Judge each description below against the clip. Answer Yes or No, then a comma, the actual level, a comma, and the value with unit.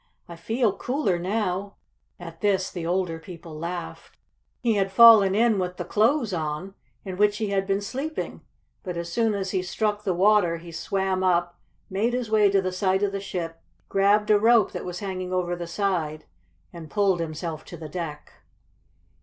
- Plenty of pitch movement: No, average, 3.1 semitones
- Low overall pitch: No, high, 190 Hz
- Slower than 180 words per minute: No, average, 185 wpm